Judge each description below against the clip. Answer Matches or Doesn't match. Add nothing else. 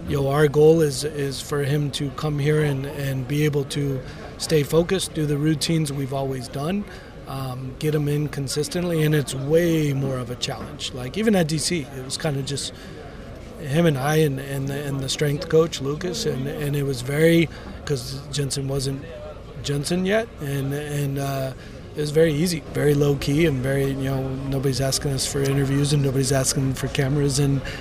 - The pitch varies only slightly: Matches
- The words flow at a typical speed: Matches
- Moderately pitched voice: Matches